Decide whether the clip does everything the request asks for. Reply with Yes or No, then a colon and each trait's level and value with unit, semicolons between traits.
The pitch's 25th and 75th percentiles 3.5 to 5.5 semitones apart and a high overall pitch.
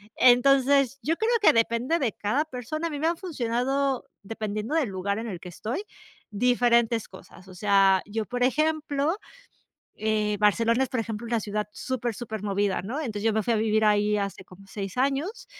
Yes: average, 4.6 semitones; high, 230 Hz